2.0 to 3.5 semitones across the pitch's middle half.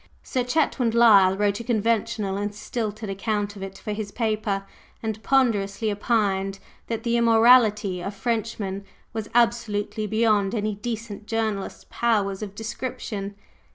Yes: narrow, 2.4 semitones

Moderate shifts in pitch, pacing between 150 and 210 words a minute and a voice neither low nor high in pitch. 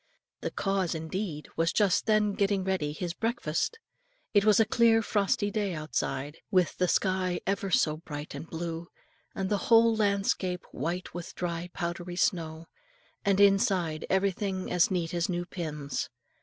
Yes: average, 3.2 semitones; average, 160 wpm; medium, 180 Hz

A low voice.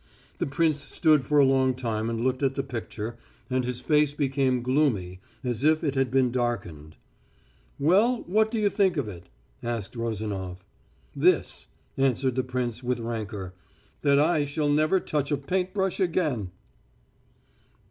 Yes: low, 130 Hz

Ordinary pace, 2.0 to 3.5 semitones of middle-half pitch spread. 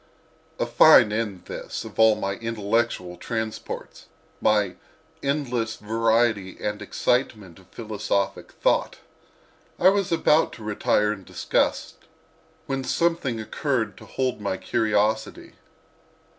No: slow, 110 wpm; average, 2.8 semitones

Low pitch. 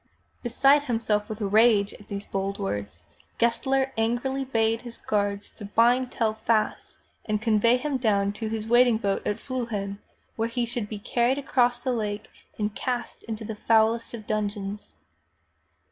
No: high, 225 Hz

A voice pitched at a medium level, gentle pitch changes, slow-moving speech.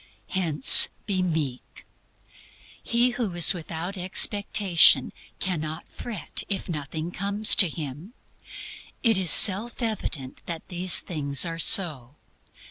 No: medium, 175 Hz; average, 4.3 semitones; slow, 115 wpm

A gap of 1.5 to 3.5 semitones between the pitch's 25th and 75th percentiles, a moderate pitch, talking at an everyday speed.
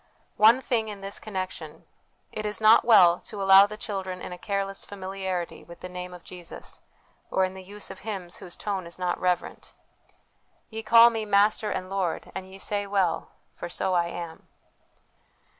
No: narrow, 2.5 semitones; high, 195 Hz; average, 185 wpm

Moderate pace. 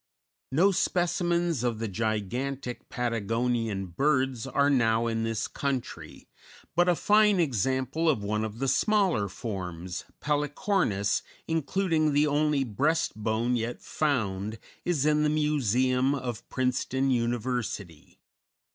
No: slow, 120 wpm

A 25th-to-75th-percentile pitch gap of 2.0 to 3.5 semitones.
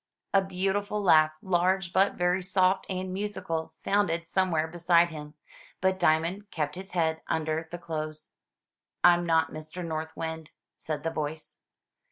Yes: average, 2.8 semitones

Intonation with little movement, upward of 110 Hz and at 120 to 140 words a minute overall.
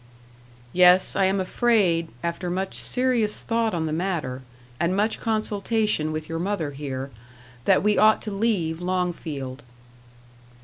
No: average, 4.7 semitones; medium, 185 Hz; slow, 135 wpm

